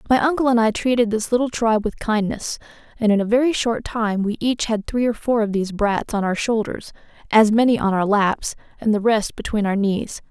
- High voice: Yes, high, 220 Hz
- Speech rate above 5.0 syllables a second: Yes, 5.4 syllables/s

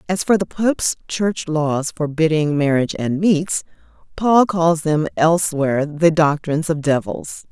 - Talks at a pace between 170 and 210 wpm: No, average, 145 wpm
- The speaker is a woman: Yes, female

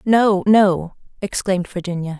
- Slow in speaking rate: Yes, slow, 110 wpm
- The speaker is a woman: Yes, female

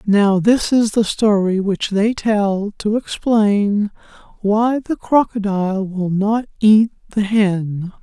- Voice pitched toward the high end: Yes, high, 210 Hz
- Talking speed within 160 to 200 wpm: No, slow, 135 wpm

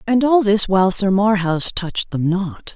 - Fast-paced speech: No, average, 195 wpm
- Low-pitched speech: No, high, 195 Hz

